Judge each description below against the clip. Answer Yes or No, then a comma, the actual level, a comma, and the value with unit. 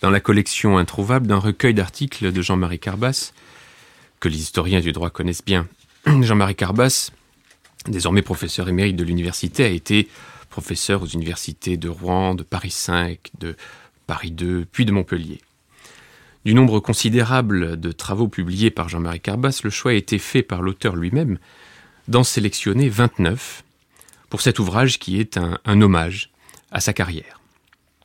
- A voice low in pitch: Yes, low, 100 Hz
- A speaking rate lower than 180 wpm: Yes, average, 150 wpm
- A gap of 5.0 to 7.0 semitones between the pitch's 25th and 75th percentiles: No, average, 4.3 semitones